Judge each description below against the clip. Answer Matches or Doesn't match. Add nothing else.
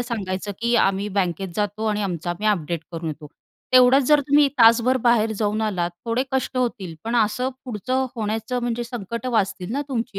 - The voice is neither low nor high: Doesn't match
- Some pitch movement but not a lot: Matches